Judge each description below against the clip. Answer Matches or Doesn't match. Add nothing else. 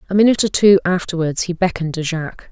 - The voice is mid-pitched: Matches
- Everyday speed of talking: Doesn't match